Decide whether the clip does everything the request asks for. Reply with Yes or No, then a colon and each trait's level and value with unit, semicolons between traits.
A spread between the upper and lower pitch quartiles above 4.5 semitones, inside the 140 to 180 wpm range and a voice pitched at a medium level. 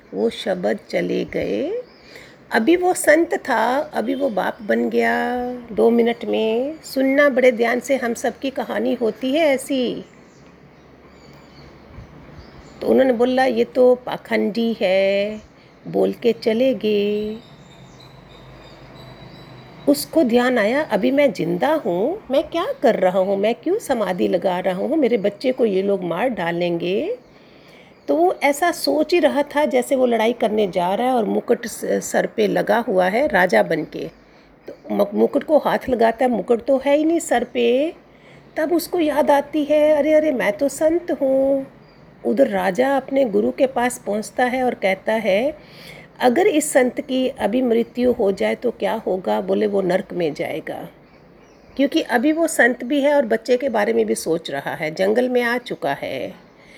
No: average, 5.0 semitones; average, 165 wpm; high, 245 Hz